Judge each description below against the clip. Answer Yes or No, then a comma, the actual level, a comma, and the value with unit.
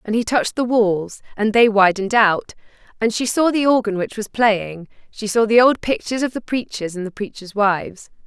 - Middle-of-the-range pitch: No, high, 220 Hz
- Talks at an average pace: No, fast, 210 wpm